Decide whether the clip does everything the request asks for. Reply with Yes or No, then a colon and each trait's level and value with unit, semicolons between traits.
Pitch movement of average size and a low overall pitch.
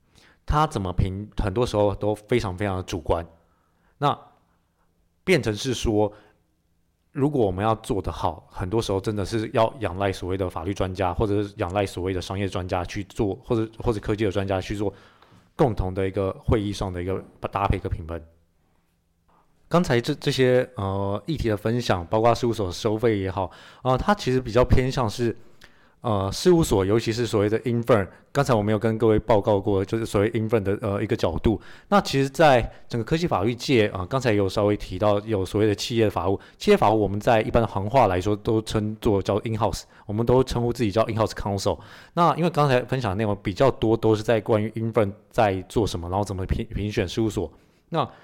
Yes: average, 3.3 semitones; low, 105 Hz